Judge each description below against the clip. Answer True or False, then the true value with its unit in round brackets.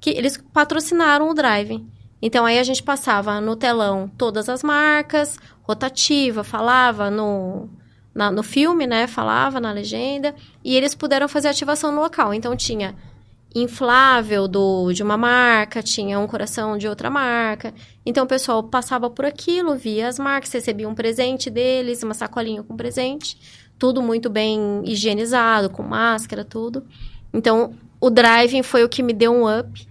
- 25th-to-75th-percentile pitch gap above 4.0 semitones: False (3.5 semitones)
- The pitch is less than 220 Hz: False (240 Hz)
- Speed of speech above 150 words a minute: True (160 wpm)